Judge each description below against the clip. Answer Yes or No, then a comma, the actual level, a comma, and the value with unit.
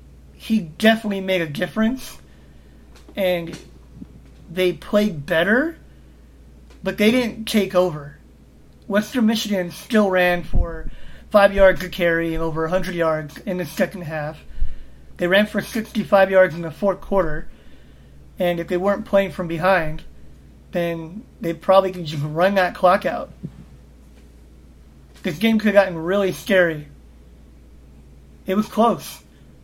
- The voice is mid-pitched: Yes, medium, 175 Hz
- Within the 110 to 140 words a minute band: Yes, slow, 135 wpm